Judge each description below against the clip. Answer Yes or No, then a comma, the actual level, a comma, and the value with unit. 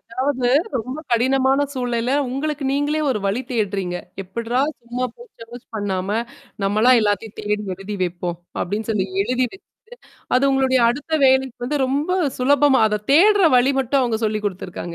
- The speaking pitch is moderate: No, high, 245 Hz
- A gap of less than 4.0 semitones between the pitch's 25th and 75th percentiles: No, average, 4.3 semitones